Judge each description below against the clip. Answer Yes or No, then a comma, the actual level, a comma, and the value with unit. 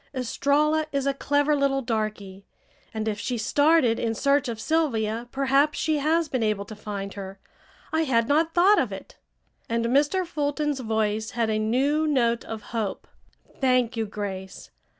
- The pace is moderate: Yes, average, 165 wpm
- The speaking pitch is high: Yes, very high, 250 Hz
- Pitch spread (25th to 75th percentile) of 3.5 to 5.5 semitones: Yes, average, 5.0 semitones